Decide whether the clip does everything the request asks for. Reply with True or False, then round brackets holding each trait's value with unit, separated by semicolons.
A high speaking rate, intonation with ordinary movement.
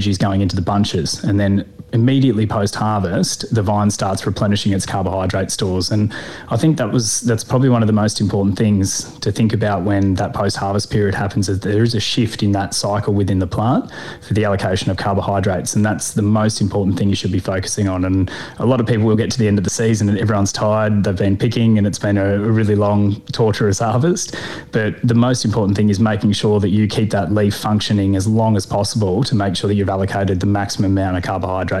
False (225 wpm; 2.0 semitones)